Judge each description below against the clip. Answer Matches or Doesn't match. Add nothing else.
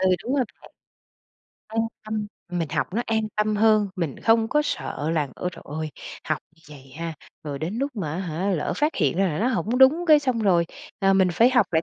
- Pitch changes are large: Matches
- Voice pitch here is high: Matches